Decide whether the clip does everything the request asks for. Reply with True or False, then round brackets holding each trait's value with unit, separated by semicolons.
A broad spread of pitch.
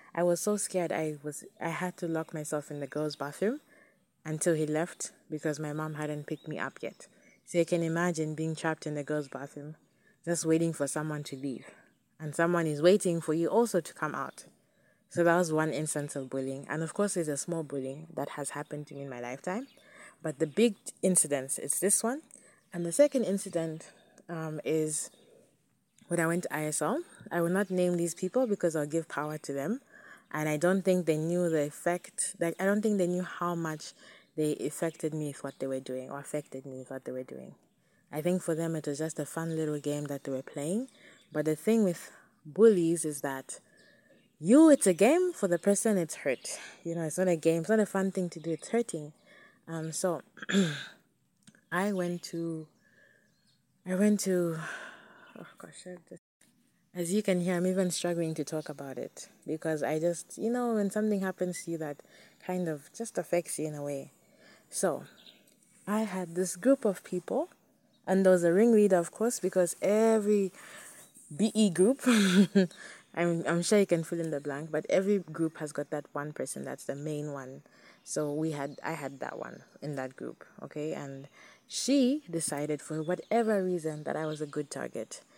False (4.1 semitones)